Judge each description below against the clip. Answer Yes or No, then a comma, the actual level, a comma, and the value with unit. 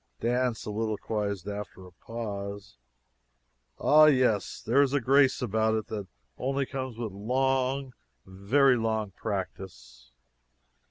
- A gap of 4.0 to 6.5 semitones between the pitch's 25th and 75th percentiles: Yes, average, 4.3 semitones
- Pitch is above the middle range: No, low, 110 Hz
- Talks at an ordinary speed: No, slow, 115 wpm